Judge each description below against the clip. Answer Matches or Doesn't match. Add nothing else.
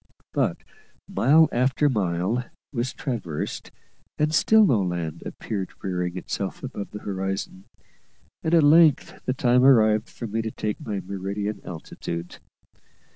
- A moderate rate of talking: Doesn't match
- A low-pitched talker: Matches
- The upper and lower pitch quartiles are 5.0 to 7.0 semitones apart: Matches